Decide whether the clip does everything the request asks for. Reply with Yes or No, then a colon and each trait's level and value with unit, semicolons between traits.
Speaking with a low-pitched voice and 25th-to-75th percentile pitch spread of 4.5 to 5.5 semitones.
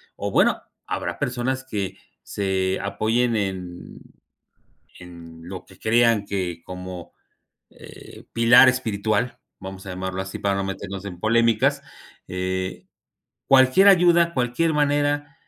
Yes: low, 100 Hz; average, 4.9 semitones